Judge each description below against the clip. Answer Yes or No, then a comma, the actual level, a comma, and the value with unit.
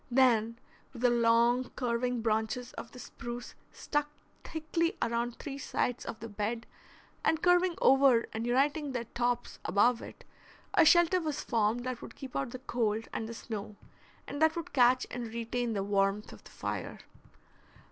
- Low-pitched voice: No, high, 240 Hz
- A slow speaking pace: No, average, 165 wpm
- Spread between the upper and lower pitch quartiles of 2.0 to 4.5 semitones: Yes, average, 2.8 semitones